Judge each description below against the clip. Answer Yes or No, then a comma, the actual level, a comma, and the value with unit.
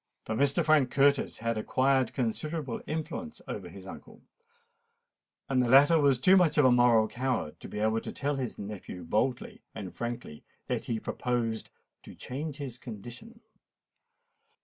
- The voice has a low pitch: Yes, low, 125 Hz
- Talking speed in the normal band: Yes, average, 155 wpm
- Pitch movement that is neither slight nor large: Yes, average, 4.0 semitones